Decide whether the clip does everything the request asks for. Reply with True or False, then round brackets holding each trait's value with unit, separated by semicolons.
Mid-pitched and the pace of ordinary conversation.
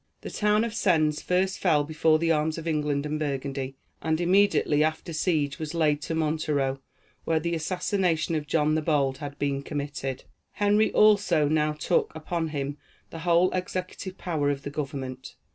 True (155 Hz; 170 wpm)